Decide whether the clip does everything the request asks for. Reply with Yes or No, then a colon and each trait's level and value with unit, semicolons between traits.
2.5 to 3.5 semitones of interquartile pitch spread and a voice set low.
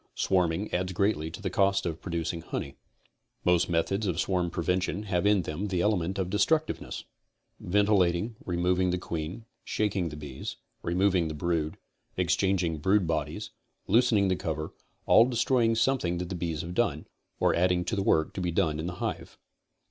Yes: average, 3.0 semitones; very low, 90 Hz